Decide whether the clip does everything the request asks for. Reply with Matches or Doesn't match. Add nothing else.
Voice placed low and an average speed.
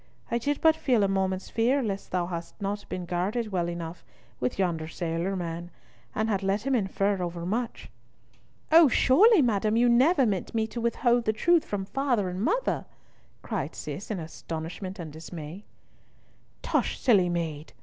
Doesn't match